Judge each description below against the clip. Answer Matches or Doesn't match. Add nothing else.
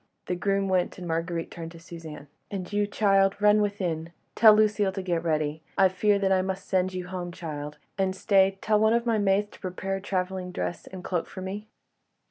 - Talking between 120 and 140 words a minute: Doesn't match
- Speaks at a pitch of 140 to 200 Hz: Matches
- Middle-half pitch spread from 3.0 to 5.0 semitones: Doesn't match